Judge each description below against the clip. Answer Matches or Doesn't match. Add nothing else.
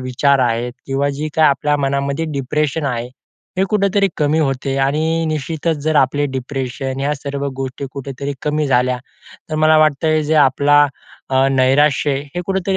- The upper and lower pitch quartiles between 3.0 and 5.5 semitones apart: Doesn't match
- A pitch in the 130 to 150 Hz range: Matches